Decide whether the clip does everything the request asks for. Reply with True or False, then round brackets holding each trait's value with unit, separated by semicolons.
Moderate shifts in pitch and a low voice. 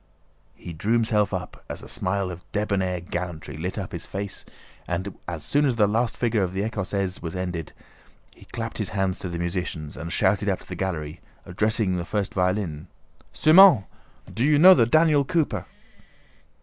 True (3.9 semitones; 95 Hz)